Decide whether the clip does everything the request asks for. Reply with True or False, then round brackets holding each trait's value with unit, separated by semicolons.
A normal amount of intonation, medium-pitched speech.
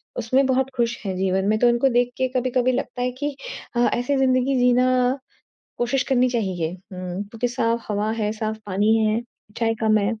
False (3.2 semitones; 235 Hz)